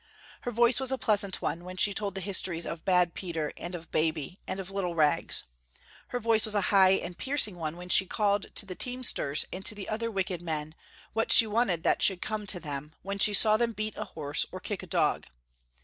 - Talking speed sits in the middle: No, fast, 225 wpm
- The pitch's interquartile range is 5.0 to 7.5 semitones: No, average, 3.8 semitones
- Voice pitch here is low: No, high, 190 Hz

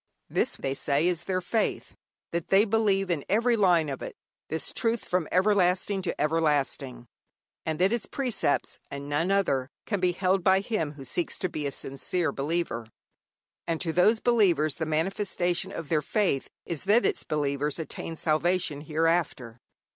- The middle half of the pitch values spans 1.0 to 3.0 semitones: No, average, 4.3 semitones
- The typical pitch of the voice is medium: Yes, medium, 170 Hz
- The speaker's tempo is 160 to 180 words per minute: Yes, average, 165 wpm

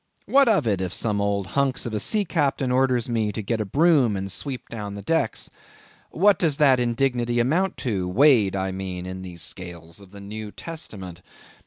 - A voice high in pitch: No, low, 110 Hz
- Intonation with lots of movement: Yes, wide, 5.9 semitones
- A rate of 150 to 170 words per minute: No, average, 195 wpm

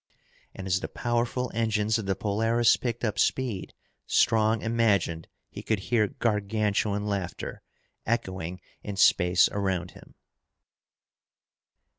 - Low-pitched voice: Yes, low, 105 Hz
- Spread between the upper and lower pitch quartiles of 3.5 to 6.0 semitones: No, average, 3.0 semitones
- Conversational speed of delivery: No, slow, 115 wpm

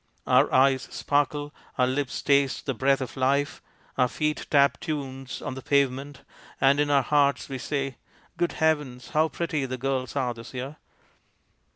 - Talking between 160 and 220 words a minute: Yes, average, 170 wpm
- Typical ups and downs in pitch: No, narrow, 1.9 semitones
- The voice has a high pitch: No, medium, 140 Hz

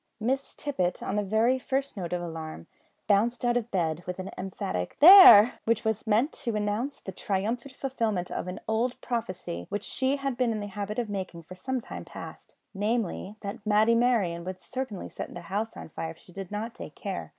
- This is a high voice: Yes, high, 210 Hz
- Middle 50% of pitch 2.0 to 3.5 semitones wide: No, average, 4.5 semitones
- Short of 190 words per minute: No, fast, 205 wpm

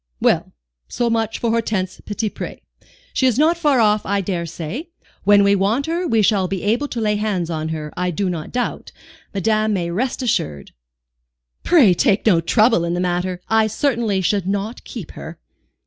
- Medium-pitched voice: No, high, 205 Hz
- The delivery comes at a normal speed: Yes, average, 180 wpm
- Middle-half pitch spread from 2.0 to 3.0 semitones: No, average, 4.2 semitones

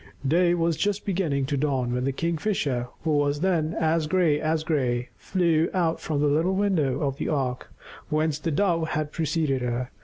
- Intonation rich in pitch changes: No, average, 3.3 semitones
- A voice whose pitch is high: No, medium, 155 Hz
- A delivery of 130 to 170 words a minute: No, average, 185 wpm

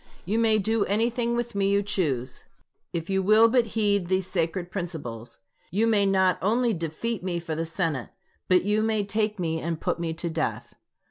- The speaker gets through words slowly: No, average, 190 wpm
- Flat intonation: No, average, 4.6 semitones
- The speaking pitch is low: No, high, 190 Hz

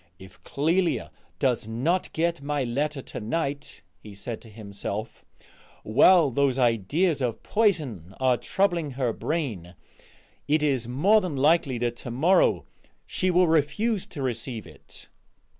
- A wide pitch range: Yes, wide, 6.1 semitones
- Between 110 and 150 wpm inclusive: Yes, average, 140 wpm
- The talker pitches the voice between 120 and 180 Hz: Yes, medium, 140 Hz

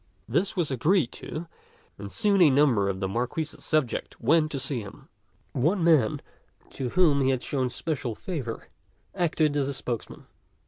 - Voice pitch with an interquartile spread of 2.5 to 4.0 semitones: No, average, 4.9 semitones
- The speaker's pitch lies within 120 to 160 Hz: Yes, medium, 140 Hz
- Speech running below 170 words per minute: Yes, average, 155 wpm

